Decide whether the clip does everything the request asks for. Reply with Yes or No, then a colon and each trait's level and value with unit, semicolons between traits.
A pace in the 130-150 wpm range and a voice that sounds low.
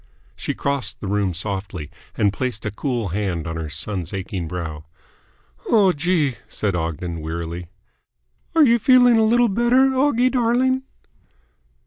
Yes: average, 140 wpm; low, 105 Hz